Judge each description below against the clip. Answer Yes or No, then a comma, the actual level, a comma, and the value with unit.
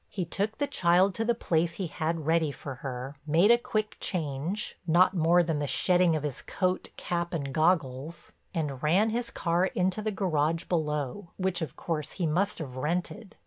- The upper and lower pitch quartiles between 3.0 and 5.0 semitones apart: Yes, average, 3.8 semitones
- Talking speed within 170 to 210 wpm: Yes, average, 180 wpm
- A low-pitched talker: No, medium, 170 Hz